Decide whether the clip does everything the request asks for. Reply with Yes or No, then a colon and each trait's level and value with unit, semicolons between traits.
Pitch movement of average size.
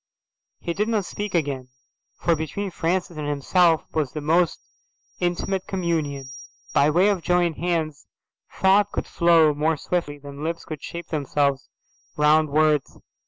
Yes: average, 3.2 semitones